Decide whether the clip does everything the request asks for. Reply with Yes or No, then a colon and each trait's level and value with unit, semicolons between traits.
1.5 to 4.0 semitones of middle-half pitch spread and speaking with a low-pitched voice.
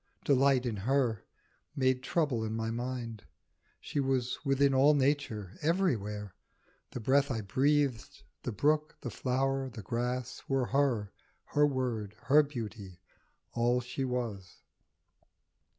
Yes: average, 3.6 semitones; low, 125 Hz